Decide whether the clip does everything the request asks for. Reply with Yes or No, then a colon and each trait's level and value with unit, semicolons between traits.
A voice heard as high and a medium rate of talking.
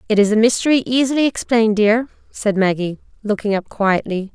Yes: high, 220 Hz; average, 165 wpm